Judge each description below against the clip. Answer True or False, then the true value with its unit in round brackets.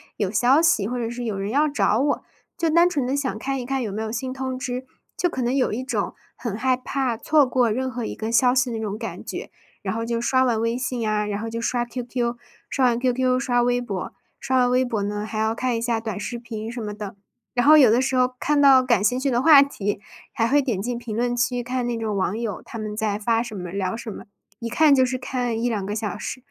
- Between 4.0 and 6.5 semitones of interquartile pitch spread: False (2.7 semitones)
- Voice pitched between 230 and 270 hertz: True (240 Hz)